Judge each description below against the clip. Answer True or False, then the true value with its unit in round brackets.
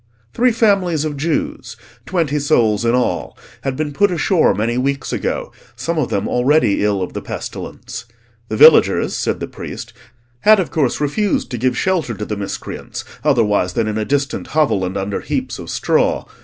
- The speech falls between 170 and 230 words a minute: True (180 wpm)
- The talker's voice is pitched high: False (140 Hz)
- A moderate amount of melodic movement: False (7.1 semitones)